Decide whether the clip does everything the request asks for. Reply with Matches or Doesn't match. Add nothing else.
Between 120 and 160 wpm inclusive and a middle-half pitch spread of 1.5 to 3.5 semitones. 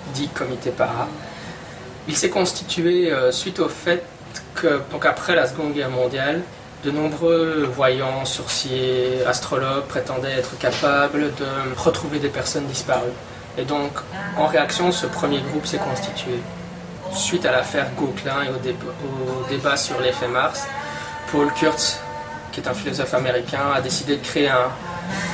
Doesn't match